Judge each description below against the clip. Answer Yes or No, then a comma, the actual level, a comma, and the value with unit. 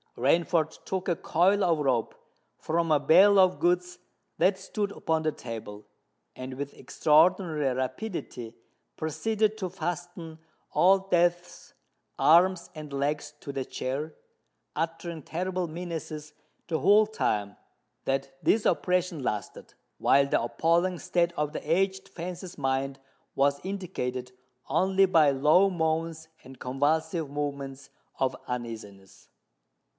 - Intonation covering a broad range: No, average, 4.7 semitones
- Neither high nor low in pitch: Yes, medium, 160 Hz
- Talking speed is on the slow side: Yes, slow, 120 wpm